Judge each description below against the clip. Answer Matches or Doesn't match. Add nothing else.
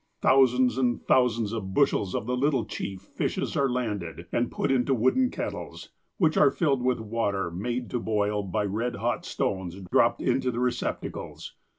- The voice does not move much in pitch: Doesn't match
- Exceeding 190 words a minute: Doesn't match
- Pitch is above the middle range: Doesn't match